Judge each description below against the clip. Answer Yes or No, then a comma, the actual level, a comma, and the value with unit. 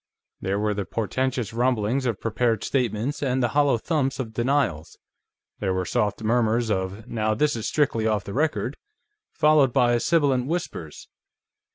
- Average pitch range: Yes, average, 4.1 semitones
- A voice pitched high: No, low, 120 Hz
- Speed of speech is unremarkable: Yes, average, 160 wpm